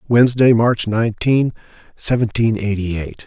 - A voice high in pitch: No, low, 110 Hz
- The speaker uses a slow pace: Yes, slow, 110 wpm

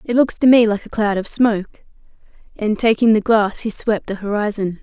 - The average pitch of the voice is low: No, high, 215 Hz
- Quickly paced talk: Yes, fast, 210 wpm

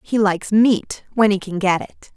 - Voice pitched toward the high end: Yes, high, 205 Hz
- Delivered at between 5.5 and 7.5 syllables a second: No, 4.6 syllables/s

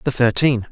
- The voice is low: Yes, low, 120 Hz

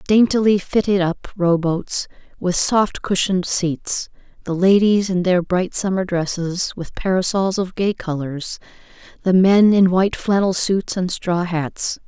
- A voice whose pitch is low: No, medium, 185 Hz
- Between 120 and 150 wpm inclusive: Yes, average, 145 wpm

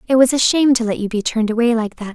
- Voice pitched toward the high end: Yes, high, 235 Hz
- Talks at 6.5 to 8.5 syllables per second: Yes, 7.4 syllables/s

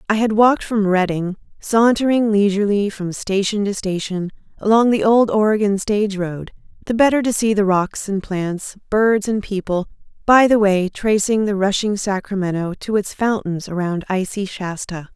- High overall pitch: Yes, high, 205 Hz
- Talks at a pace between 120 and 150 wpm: No, average, 160 wpm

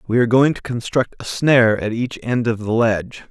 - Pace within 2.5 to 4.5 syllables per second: No, 5.6 syllables/s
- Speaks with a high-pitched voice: No, low, 120 Hz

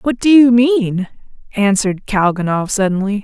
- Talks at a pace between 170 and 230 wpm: No, slow, 130 wpm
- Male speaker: No, female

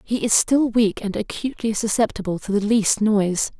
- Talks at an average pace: Yes, average, 185 wpm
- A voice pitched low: No, high, 215 Hz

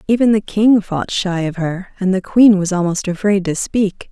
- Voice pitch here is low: No, high, 195 Hz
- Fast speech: Yes, fast, 220 wpm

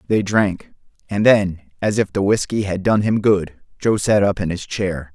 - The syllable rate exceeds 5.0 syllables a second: No, 4.4 syllables/s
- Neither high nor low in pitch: No, low, 100 Hz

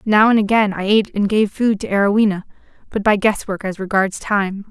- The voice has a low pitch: No, high, 205 Hz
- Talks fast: Yes, fast, 215 wpm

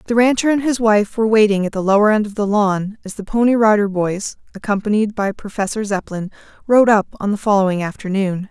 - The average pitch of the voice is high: Yes, high, 210 Hz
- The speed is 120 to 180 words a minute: No, fast, 205 wpm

